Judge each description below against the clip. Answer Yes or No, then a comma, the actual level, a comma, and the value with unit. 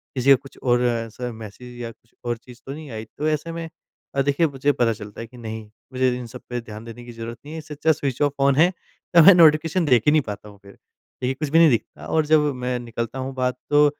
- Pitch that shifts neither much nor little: Yes, average, 4.2 semitones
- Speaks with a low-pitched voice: Yes, low, 130 Hz